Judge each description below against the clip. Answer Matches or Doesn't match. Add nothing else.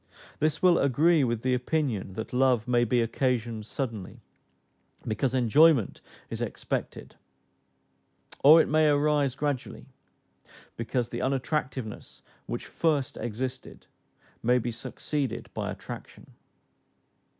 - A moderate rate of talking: Doesn't match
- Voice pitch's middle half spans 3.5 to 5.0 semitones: Matches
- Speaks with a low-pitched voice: Matches